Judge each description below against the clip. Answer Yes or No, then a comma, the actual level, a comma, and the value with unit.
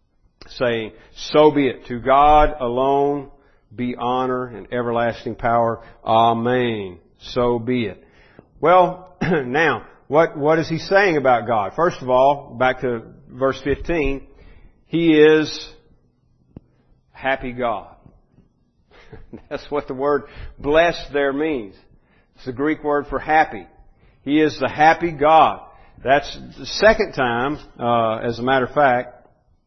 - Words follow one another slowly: Yes, slow, 130 wpm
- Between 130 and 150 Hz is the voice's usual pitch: Yes, low, 135 Hz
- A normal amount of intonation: Yes, average, 4.1 semitones